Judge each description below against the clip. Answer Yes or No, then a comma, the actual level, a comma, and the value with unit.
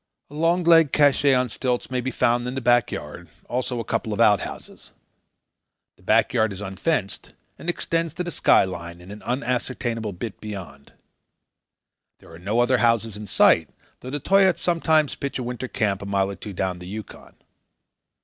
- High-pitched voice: No, low, 120 Hz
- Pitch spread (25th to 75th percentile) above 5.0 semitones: Yes, wide, 5.4 semitones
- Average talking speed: Yes, average, 180 wpm